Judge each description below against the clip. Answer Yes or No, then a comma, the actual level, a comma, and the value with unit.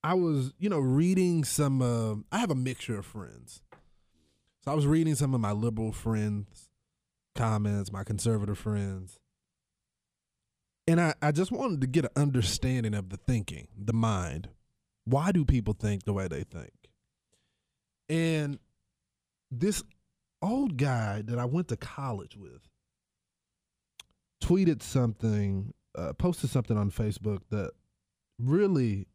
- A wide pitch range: Yes, wide, 6.2 semitones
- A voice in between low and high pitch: No, low, 120 Hz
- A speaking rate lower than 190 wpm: Yes, average, 140 wpm